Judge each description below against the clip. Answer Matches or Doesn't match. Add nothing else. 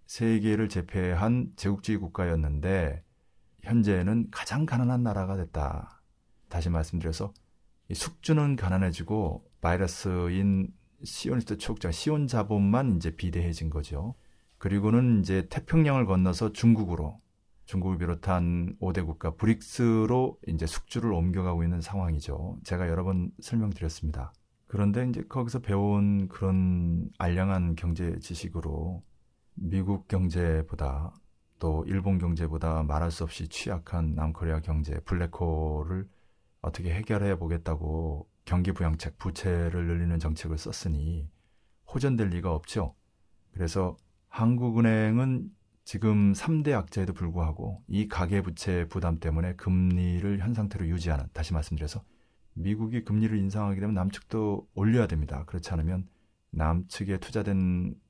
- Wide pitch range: Doesn't match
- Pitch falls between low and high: Doesn't match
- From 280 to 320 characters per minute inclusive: Matches